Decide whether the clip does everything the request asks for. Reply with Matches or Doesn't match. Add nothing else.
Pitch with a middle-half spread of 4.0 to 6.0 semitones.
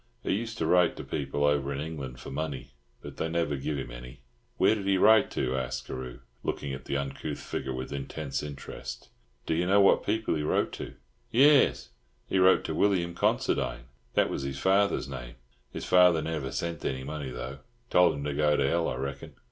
Matches